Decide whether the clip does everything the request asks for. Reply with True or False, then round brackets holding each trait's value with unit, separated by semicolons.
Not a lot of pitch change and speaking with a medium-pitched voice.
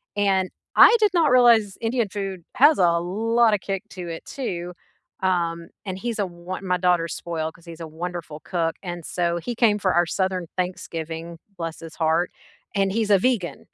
False (3.4 semitones; 180 Hz)